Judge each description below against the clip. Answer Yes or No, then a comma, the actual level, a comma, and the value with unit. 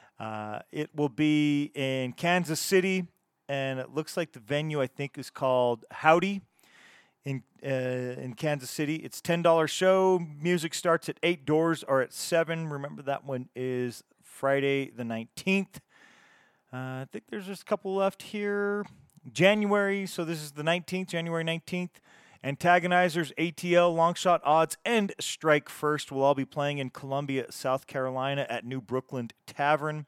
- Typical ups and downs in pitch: Yes, average, 4.5 semitones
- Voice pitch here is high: No, medium, 150 Hz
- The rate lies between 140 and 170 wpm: Yes, average, 155 wpm